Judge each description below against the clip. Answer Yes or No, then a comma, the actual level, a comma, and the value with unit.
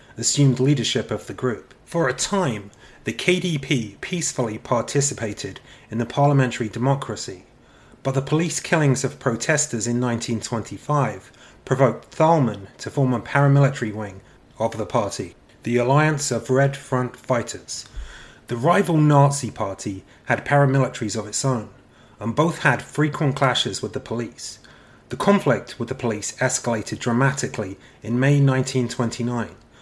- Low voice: Yes, low, 125 Hz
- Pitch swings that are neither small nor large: Yes, average, 3.4 semitones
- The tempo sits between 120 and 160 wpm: Yes, slow, 135 wpm